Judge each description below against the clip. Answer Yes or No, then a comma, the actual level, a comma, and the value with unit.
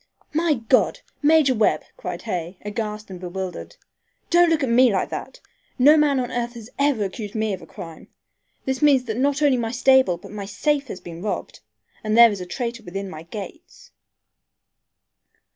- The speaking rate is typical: Yes, average, 180 wpm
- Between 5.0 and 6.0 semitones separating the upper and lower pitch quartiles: Yes, wide, 5.6 semitones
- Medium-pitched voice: No, high, 230 Hz